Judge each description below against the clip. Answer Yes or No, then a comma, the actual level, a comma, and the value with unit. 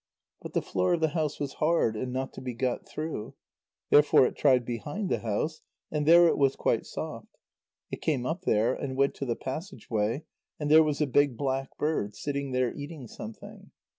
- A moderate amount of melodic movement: Yes, average, 3.6 semitones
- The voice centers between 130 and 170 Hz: Yes, medium, 140 Hz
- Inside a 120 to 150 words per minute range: No, average, 200 wpm